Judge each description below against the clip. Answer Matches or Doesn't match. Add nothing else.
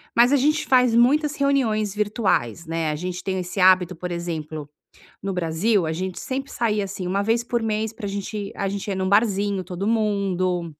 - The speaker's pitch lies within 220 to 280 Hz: Doesn't match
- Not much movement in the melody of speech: Doesn't match